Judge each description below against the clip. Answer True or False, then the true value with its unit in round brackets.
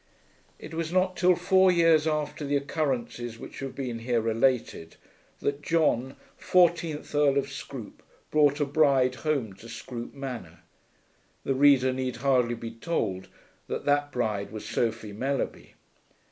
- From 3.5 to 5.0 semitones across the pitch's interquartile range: True (4.4 semitones)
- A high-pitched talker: False (135 Hz)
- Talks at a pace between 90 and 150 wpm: True (145 wpm)